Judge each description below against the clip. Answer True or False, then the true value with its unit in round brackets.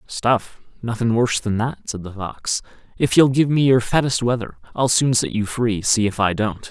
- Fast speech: True (215 wpm)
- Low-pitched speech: True (115 Hz)